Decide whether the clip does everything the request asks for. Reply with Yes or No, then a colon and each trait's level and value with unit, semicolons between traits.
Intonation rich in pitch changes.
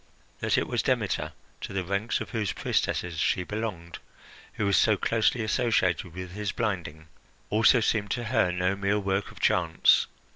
No: average, 3.2 semitones